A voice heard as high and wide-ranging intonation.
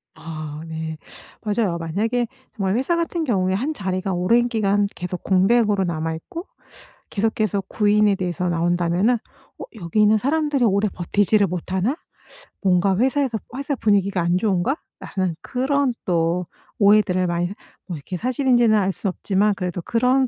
No: high, 200 Hz; average, 4.7 semitones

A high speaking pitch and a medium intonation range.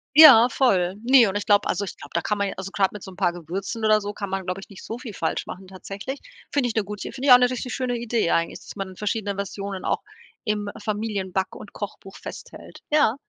Yes: high, 205 Hz; average, 3.0 semitones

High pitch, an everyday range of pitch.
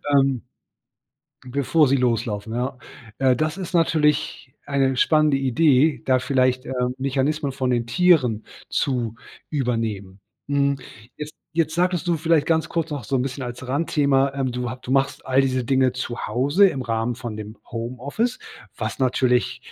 No: low, 135 Hz; average, 3.2 semitones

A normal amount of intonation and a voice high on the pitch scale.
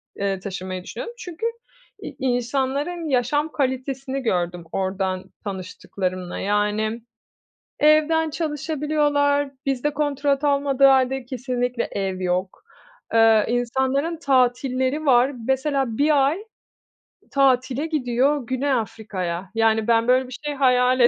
Yes: average, 4.3 semitones; very high, 260 Hz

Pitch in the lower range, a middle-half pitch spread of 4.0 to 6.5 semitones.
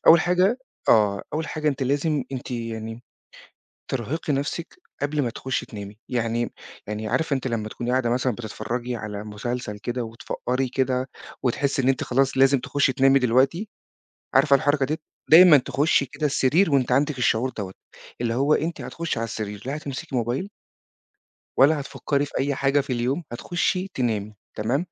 No: low, 130 Hz; average, 3.5 semitones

